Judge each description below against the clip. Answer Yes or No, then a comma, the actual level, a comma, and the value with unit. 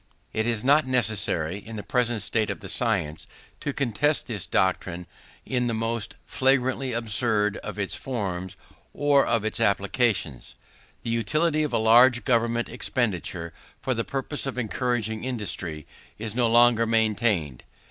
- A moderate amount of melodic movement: Yes, average, 3.4 semitones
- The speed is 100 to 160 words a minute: Yes, average, 145 wpm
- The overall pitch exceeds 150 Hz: No, low, 115 Hz